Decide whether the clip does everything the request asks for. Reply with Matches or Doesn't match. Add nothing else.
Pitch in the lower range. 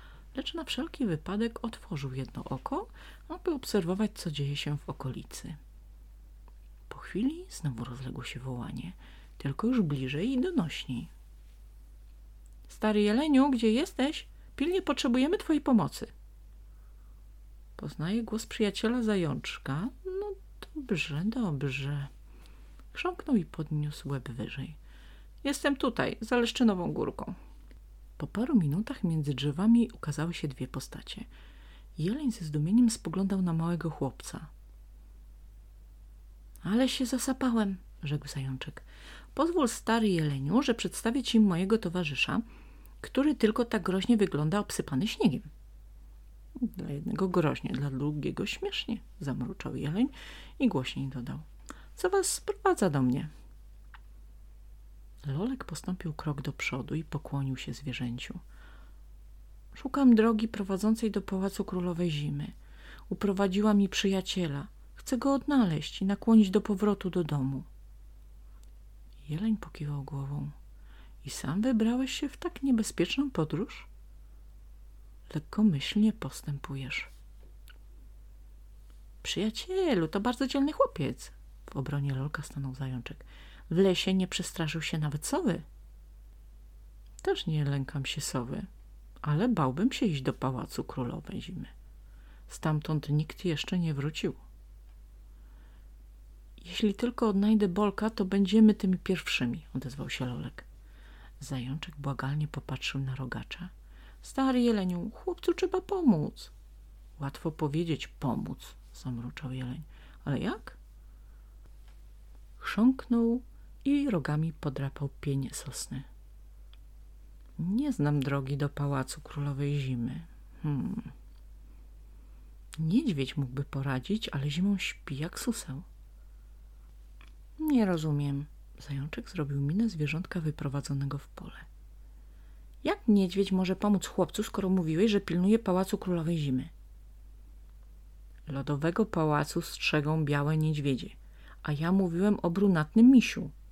Doesn't match